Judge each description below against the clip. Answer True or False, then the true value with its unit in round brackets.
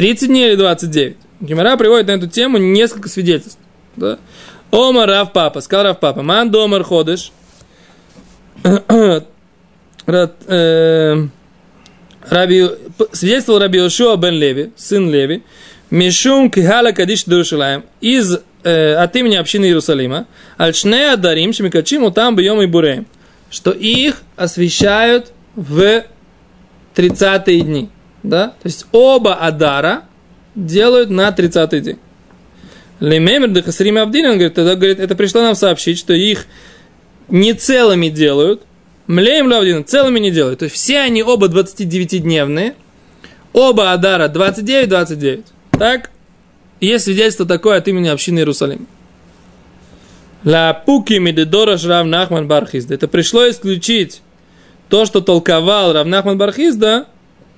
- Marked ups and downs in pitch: False (4.3 semitones)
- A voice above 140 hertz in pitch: True (190 Hz)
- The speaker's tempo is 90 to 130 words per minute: True (115 wpm)